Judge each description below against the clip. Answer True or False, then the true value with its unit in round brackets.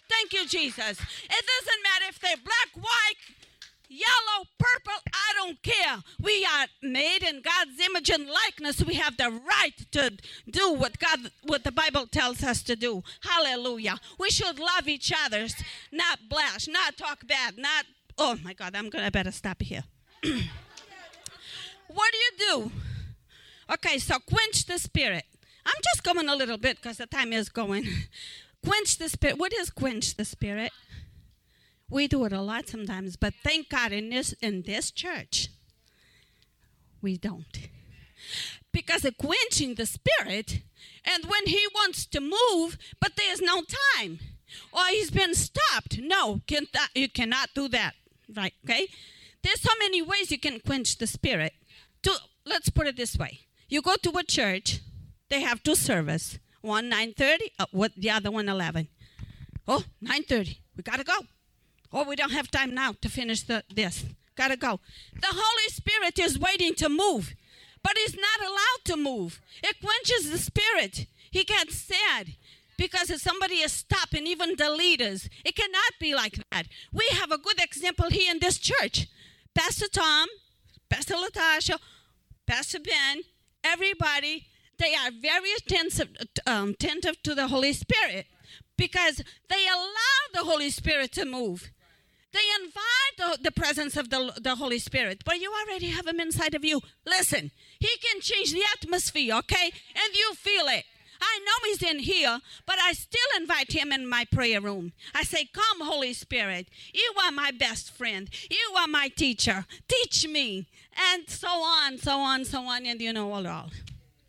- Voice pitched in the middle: False (315 Hz)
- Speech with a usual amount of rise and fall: False (7.3 semitones)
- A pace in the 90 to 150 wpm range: False (175 wpm)